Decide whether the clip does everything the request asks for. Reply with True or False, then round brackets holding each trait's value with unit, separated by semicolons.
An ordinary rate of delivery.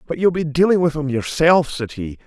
False (240 wpm)